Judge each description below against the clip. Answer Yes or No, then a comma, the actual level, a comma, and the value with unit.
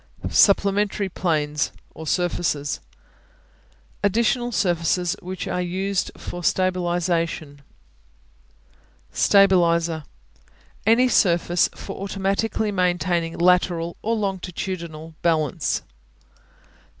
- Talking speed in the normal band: No, slow, 75 wpm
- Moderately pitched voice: Yes, medium, 180 Hz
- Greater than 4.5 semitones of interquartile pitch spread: No, average, 2.7 semitones